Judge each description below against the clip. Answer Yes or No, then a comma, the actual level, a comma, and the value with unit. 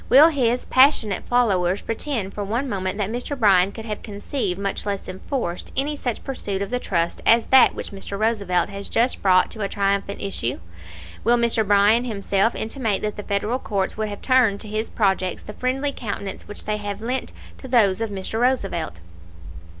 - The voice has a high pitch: Yes, high, 210 Hz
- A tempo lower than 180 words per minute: No, average, 190 wpm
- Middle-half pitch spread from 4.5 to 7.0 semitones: No, average, 3.5 semitones